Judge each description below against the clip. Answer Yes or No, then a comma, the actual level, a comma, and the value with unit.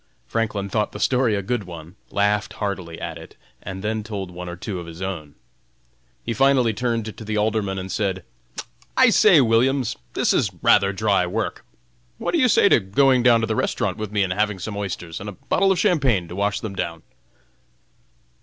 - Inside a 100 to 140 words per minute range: No, average, 200 wpm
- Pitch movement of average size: Yes, average, 3.3 semitones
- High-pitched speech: No, low, 105 Hz